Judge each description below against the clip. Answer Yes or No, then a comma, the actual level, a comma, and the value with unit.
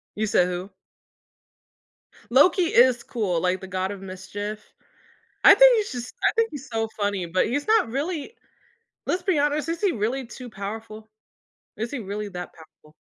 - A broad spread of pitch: Yes, wide, 6.9 semitones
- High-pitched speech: Yes, high, 225 Hz